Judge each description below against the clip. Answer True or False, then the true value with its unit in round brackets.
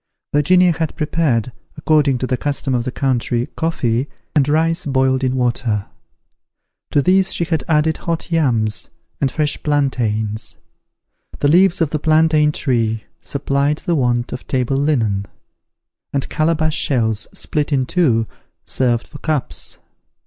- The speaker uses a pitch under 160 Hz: True (140 Hz)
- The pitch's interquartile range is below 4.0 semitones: False (4.3 semitones)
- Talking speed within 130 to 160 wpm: True (140 wpm)